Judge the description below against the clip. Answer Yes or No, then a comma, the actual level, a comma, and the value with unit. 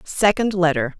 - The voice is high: No, medium, 175 Hz